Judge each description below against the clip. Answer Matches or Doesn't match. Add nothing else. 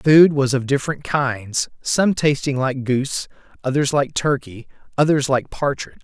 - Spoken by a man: Matches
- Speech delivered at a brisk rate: Doesn't match